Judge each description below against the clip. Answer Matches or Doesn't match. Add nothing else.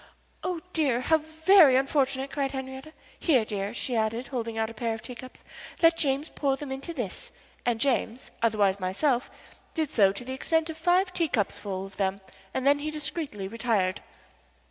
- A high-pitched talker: Matches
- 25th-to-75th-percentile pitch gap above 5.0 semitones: Matches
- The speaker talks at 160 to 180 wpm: Matches